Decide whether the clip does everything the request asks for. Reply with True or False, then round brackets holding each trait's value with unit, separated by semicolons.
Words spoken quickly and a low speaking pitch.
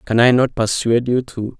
True (225 wpm; 120 Hz)